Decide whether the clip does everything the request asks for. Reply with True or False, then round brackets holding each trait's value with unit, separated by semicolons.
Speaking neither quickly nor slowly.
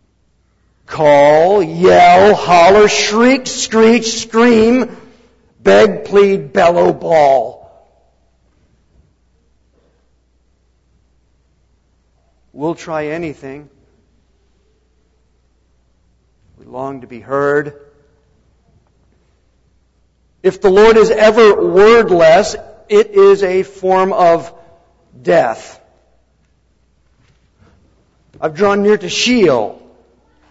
False (70 wpm)